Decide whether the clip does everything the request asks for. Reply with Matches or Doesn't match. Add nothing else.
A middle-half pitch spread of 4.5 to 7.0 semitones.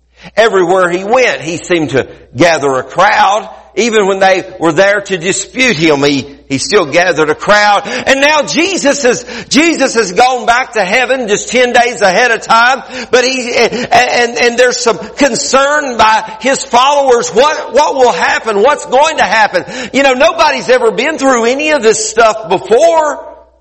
Matches